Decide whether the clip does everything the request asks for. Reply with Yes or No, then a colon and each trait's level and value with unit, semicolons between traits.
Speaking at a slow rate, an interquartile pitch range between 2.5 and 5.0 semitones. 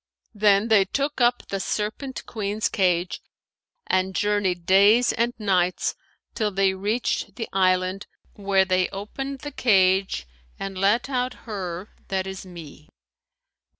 Yes: slow, 130 wpm; average, 2.8 semitones